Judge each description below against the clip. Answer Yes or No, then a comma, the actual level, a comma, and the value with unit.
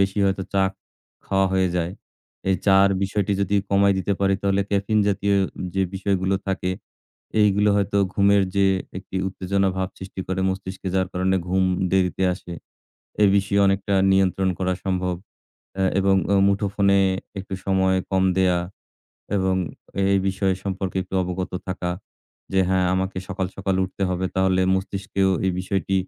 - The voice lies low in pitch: Yes, very low, 95 Hz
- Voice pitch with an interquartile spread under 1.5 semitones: Yes, narrow, 0.9 semitones